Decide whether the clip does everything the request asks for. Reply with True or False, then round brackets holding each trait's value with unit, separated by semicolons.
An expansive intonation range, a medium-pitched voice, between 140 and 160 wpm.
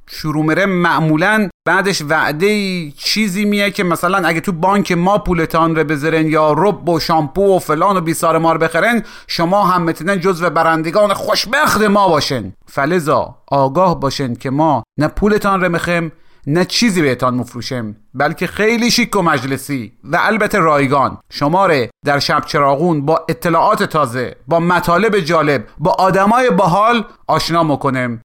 False (4.6 semitones; 165 Hz; 155 wpm)